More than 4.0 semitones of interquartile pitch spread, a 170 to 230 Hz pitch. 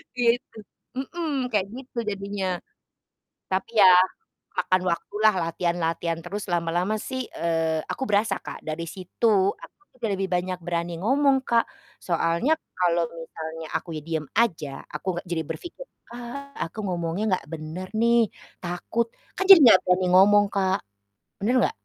Yes: average, 5.2 semitones; medium, 185 Hz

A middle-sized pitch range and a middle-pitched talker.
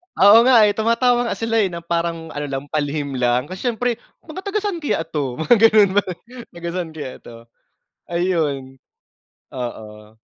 No: wide, 8.2 semitones; medium, 170 Hz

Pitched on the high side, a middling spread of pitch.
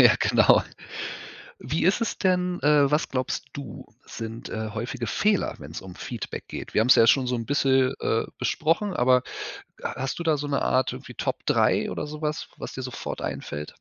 No: low, 135 Hz; average, 4.1 semitones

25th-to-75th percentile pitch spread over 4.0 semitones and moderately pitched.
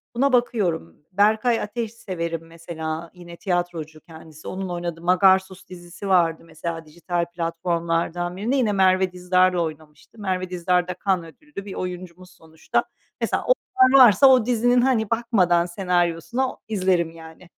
No: average, 3.4 semitones; medium, 180 Hz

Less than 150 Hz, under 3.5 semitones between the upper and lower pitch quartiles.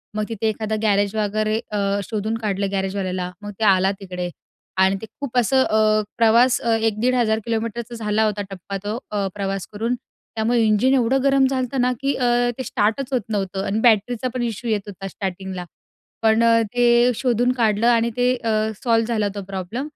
No: high, 220 Hz; average, 2.9 semitones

